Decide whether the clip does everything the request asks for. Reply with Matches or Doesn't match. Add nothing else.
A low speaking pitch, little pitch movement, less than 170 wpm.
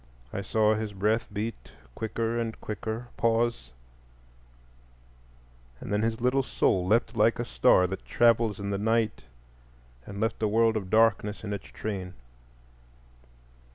Matches